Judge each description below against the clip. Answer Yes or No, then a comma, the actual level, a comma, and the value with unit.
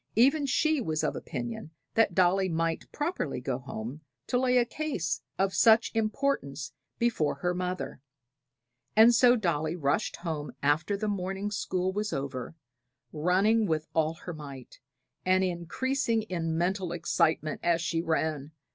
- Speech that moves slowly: No, average, 145 wpm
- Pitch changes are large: Yes, wide, 5.8 semitones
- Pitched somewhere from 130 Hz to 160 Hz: No, medium, 180 Hz